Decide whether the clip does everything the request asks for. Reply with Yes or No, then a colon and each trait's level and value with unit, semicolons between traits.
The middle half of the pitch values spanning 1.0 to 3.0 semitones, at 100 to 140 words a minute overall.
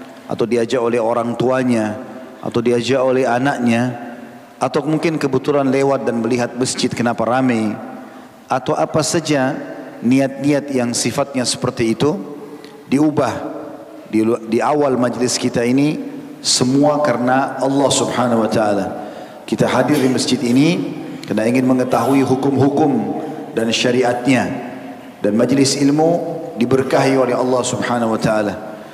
Yes: narrow, 2.6 semitones; average, 120 wpm